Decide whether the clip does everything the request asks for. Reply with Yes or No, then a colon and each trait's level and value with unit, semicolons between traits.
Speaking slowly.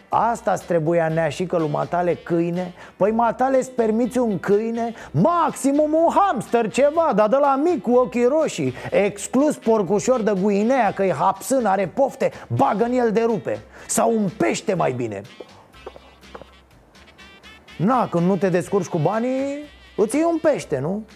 No: average, 155 wpm